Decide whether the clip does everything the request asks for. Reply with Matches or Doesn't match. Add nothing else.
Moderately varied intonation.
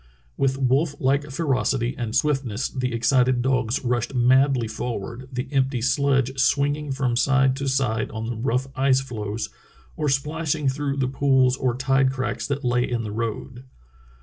Doesn't match